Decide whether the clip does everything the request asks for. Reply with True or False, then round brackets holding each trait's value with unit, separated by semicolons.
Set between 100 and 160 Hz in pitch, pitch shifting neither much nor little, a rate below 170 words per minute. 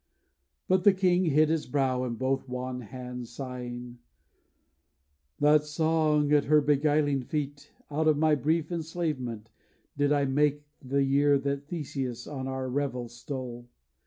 True (140 Hz; 3.0 semitones; 140 wpm)